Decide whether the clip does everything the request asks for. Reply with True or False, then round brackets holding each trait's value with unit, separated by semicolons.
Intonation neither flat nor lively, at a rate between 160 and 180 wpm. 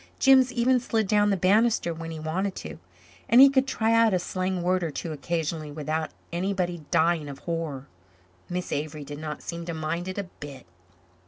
False (4.4 semitones; 190 wpm)